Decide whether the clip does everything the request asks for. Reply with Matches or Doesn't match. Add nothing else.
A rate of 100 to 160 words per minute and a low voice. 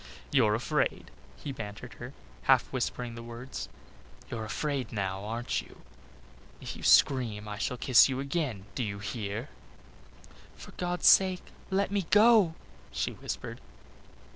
Matches